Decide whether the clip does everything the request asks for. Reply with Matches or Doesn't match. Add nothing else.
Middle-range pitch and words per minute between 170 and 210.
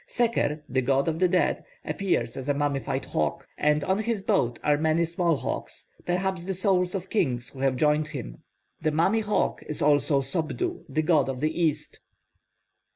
Matches